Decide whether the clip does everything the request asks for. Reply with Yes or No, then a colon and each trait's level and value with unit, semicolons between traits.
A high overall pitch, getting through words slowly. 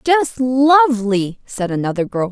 Yes: high, 235 Hz; slow, 130 wpm